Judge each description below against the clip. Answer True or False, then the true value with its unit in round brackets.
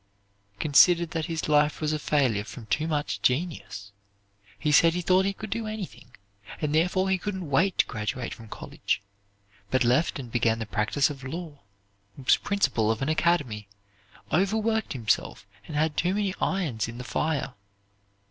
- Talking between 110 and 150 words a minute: False (165 wpm)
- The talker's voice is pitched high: False (150 Hz)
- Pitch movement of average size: False (6.2 semitones)